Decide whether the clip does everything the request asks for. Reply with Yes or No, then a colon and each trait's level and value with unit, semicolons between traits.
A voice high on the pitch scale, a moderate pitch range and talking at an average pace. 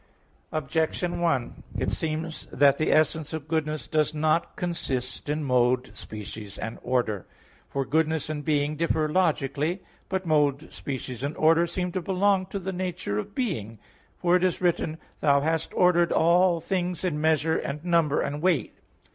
No: medium, 155 Hz; average, 3.5 semitones; average, 165 wpm